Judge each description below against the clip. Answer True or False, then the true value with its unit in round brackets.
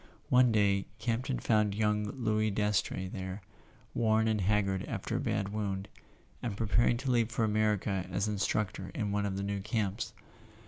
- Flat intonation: True (2.1 semitones)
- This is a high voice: False (105 Hz)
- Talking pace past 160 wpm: True (170 wpm)